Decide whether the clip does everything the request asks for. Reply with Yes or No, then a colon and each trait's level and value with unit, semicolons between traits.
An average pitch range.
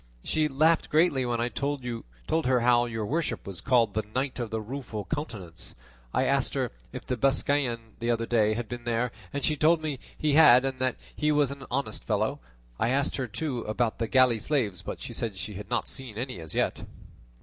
Yes: average, 3.9 semitones